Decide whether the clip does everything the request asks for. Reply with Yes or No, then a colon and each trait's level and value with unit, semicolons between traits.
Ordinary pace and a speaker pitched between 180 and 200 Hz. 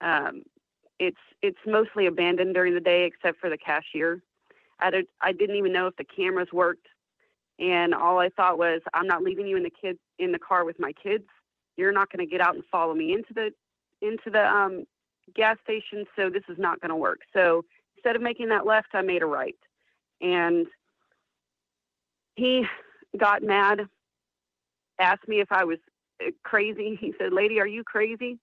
Yes: average, 190 wpm; high, 190 Hz